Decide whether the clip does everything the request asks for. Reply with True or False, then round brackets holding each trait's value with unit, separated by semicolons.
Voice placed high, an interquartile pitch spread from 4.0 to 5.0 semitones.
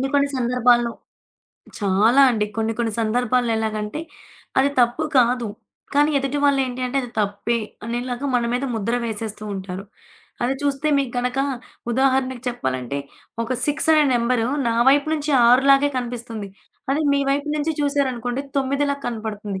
False (245 Hz; 3.4 semitones)